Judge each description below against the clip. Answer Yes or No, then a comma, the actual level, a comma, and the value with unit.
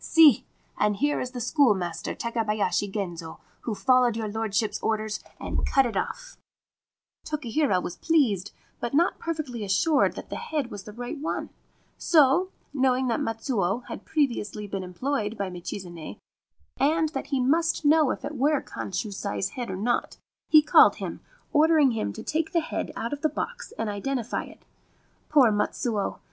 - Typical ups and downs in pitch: No, wide, 6.1 semitones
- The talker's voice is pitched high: Yes, high, 240 Hz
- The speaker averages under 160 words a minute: No, average, 165 wpm